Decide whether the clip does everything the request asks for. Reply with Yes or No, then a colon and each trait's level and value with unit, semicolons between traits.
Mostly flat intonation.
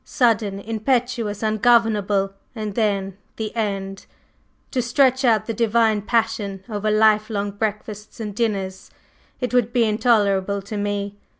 Yes: narrow, 2.2 semitones